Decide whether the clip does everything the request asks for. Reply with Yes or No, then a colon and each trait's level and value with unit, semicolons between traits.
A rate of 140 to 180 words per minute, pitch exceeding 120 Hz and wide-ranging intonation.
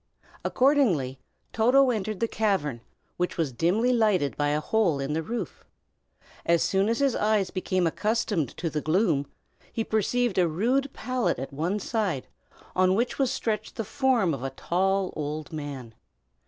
Yes: average, 160 wpm; high, 190 Hz; wide, 6.7 semitones